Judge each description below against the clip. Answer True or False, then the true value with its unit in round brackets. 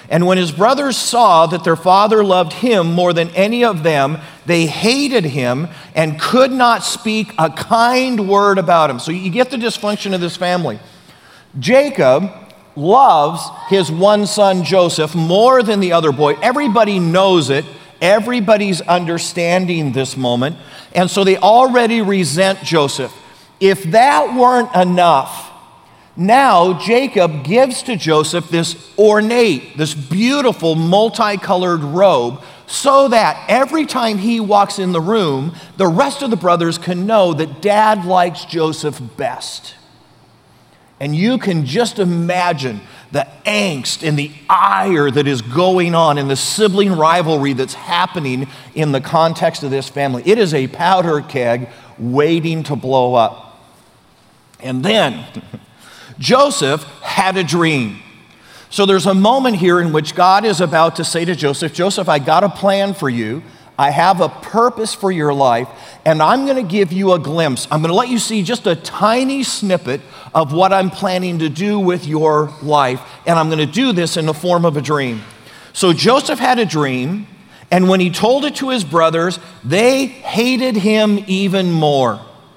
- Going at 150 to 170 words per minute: True (160 wpm)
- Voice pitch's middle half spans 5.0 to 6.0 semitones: True (5.3 semitones)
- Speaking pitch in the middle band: True (180 Hz)